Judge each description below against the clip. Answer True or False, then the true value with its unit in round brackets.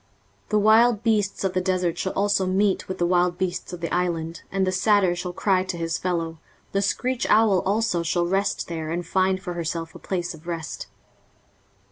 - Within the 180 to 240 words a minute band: True (200 wpm)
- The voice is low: False (185 Hz)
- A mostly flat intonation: True (2.3 semitones)